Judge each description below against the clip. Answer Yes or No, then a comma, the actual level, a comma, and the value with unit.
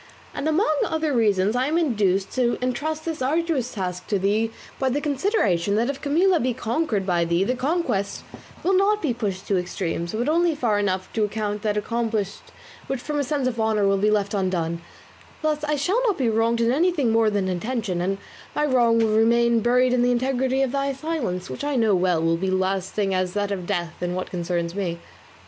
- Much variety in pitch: Yes, wide, 6.1 semitones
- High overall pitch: Yes, high, 225 Hz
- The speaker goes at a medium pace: No, fast, 210 wpm